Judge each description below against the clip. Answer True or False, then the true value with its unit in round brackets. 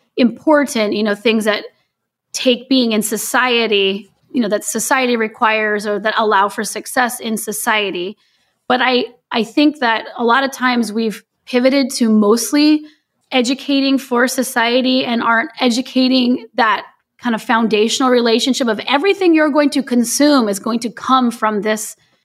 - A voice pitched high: True (235 Hz)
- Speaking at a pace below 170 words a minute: True (155 wpm)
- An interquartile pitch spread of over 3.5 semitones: False (3.0 semitones)